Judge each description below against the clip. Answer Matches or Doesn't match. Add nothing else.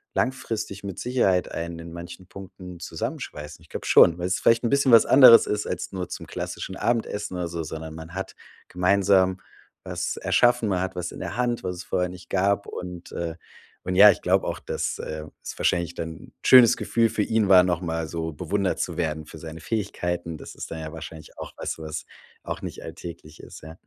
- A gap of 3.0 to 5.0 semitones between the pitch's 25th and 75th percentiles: Matches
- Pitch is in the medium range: Doesn't match